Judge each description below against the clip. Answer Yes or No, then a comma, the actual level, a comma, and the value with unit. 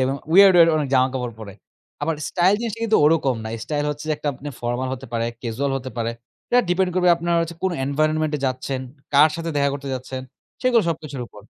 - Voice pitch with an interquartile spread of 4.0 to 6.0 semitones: Yes, average, 4.4 semitones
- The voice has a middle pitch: Yes, medium, 145 Hz